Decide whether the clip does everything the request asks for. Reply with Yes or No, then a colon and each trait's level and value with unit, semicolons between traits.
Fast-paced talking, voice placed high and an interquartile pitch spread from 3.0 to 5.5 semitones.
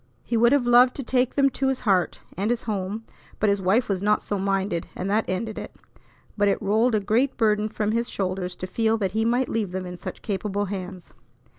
Yes: fast, 230 wpm; high, 210 Hz; average, 3.3 semitones